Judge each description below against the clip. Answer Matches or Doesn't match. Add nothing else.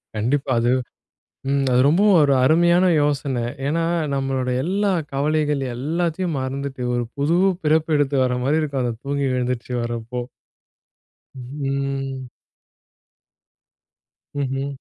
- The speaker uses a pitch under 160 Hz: Matches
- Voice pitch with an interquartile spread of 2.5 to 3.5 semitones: Matches